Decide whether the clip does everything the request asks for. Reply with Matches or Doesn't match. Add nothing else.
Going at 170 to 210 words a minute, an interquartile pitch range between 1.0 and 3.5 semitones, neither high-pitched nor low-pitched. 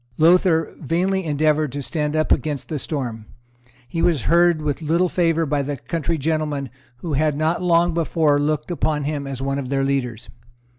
Matches